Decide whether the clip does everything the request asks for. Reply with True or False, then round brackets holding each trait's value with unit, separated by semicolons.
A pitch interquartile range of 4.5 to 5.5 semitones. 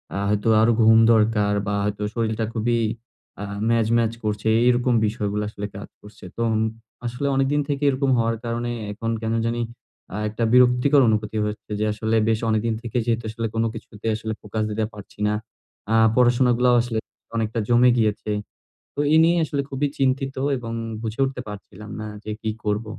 False (2.4 semitones)